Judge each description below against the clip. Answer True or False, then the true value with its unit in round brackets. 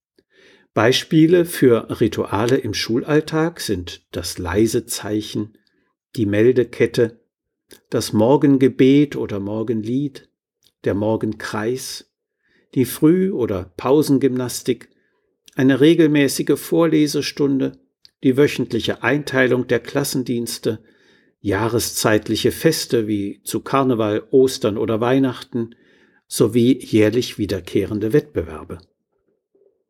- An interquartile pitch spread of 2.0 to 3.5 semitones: False (4.8 semitones)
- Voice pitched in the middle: False (125 Hz)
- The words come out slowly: True (80 wpm)